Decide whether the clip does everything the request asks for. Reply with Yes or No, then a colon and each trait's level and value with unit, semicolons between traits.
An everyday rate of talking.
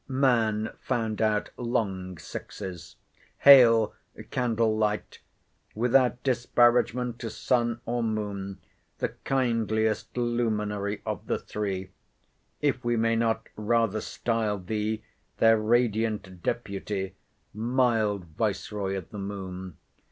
No: slow, 100 wpm